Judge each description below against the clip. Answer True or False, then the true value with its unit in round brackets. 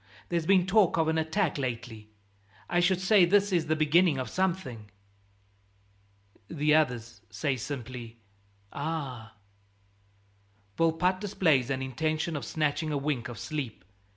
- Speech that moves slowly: True (130 wpm)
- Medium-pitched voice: True (155 Hz)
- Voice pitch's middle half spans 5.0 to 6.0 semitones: True (5.3 semitones)